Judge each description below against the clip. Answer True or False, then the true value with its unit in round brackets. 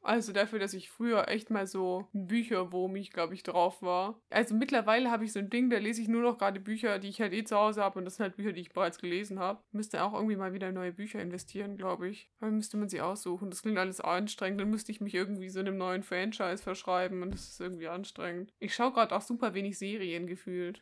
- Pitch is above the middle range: True (195 Hz)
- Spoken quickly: True (255 wpm)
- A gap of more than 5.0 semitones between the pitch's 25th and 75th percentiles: False (2.7 semitones)